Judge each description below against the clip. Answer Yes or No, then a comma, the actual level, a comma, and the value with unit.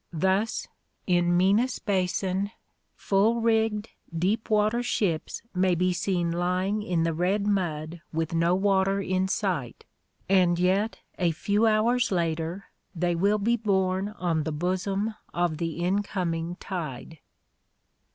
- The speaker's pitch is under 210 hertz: Yes, medium, 185 Hz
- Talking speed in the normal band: No, slow, 130 wpm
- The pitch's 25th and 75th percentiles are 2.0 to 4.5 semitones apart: Yes, average, 3.0 semitones